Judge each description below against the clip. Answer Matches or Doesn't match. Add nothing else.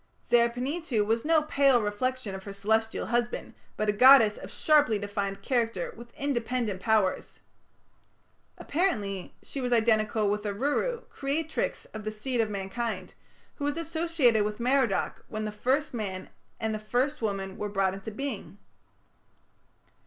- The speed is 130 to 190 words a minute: Matches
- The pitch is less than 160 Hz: Doesn't match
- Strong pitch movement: Doesn't match